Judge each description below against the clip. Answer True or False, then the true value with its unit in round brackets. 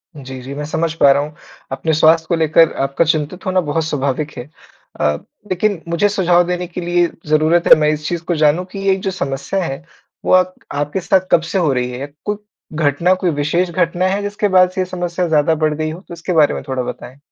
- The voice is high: False (165 Hz)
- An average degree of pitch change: True (3.6 semitones)